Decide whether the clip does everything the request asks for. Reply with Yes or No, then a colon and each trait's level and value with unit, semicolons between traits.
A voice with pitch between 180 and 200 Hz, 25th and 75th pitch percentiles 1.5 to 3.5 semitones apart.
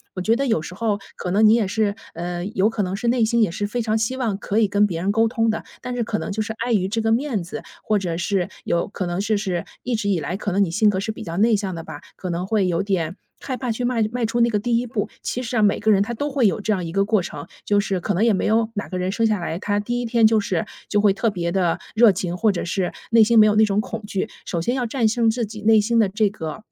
No: high, 210 Hz; average, 3.1 semitones